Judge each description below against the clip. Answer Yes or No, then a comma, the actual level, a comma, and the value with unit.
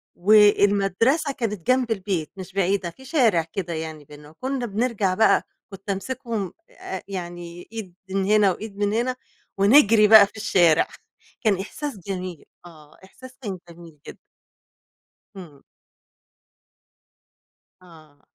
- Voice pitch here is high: Yes, high, 195 Hz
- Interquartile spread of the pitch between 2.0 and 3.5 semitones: No, average, 4.2 semitones